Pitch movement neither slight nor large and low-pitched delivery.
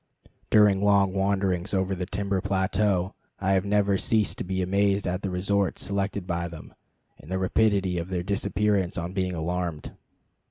No: narrow, 1.8 semitones; very low, 95 Hz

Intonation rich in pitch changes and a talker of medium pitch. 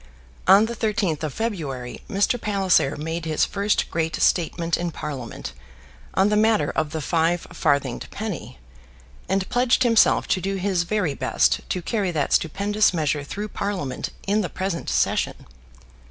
No: average, 4.7 semitones; medium, 180 Hz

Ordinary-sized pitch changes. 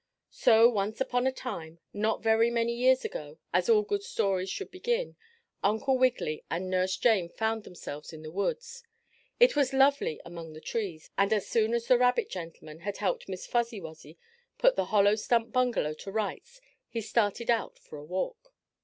No: wide, 5.7 semitones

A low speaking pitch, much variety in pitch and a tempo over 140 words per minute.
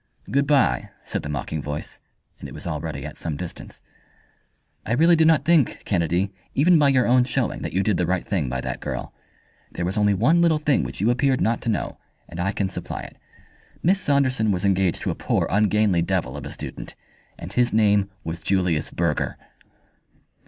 Yes: low, 105 Hz; wide, 7.2 semitones; average, 200 wpm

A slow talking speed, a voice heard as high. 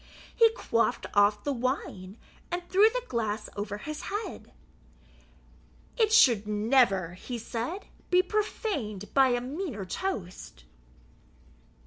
Yes: slow, 115 wpm; high, 245 Hz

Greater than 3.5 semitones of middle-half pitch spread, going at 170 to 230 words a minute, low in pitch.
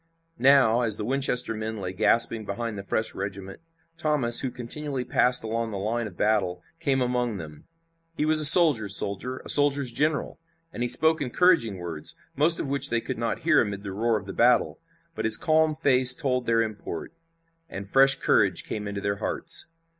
Yes: average, 4.9 semitones; average, 190 wpm; low, 120 Hz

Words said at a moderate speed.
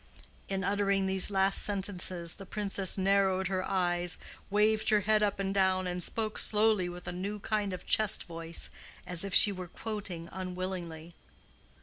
Yes: average, 165 wpm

